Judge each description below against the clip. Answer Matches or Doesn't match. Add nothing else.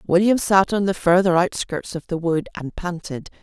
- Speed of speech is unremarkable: Matches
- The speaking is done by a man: Doesn't match